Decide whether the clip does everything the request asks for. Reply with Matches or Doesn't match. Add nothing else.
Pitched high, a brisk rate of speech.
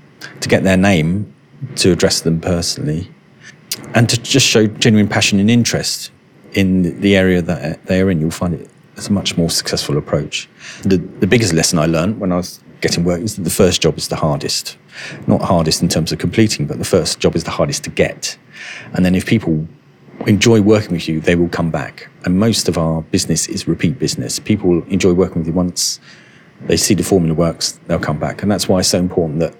Doesn't match